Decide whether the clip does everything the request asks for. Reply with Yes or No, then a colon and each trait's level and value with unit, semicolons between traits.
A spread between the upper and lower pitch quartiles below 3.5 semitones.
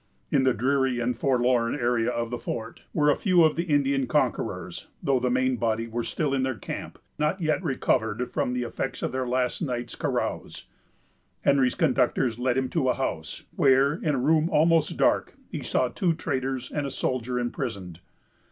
Yes: average, 2.9 semitones